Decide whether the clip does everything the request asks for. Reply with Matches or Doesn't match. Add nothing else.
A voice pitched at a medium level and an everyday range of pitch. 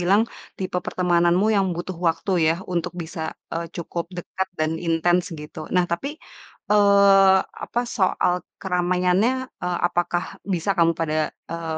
Doesn't match